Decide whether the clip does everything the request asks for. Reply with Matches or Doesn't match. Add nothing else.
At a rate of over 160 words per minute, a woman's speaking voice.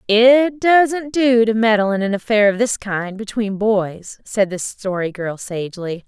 Matches